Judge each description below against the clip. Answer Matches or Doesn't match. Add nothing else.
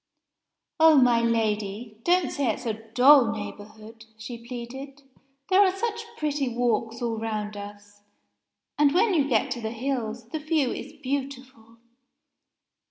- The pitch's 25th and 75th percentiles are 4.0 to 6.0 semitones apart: Matches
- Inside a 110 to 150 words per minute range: Matches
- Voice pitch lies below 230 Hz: Doesn't match